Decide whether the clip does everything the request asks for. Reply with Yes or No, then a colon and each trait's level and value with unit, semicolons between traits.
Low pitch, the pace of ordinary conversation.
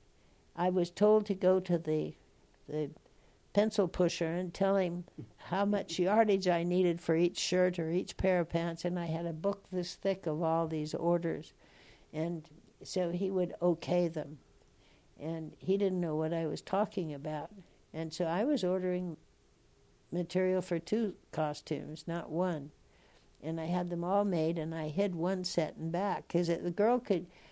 No: medium, 175 Hz; average, 175 wpm